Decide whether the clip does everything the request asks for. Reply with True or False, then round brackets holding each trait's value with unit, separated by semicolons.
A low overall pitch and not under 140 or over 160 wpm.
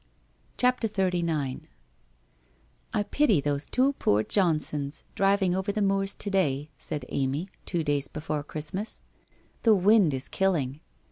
False (170 Hz; 145 wpm)